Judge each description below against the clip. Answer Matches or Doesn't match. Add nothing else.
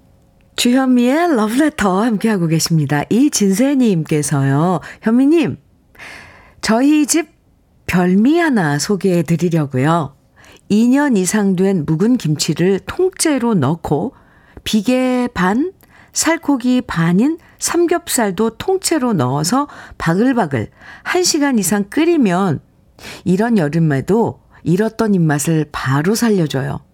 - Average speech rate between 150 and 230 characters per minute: Matches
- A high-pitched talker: Matches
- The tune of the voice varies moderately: Doesn't match